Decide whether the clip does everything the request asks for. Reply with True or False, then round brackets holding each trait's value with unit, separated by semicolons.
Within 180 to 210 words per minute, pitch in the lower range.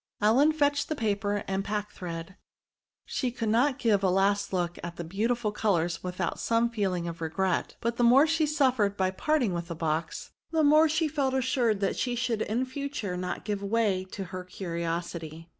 False (185 wpm; 205 Hz)